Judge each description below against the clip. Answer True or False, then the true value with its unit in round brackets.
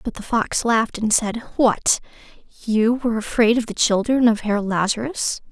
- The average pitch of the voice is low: False (225 Hz)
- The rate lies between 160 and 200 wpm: True (175 wpm)